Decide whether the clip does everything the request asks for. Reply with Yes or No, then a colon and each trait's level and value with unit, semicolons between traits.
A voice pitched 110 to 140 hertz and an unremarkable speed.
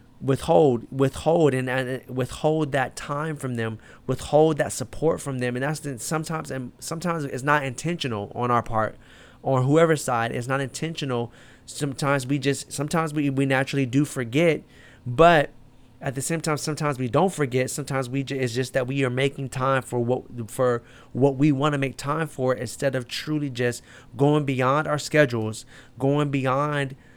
Yes: low, 135 Hz; average, 175 wpm